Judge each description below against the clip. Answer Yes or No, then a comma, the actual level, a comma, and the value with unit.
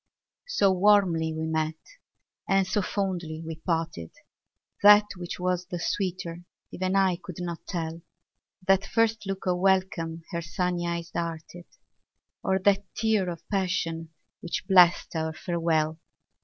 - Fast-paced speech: No, slow, 135 wpm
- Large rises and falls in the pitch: No, narrow, 2.6 semitones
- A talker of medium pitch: Yes, medium, 175 Hz